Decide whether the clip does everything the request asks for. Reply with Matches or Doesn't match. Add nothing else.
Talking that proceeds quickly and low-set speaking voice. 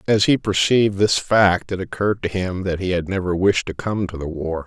Matches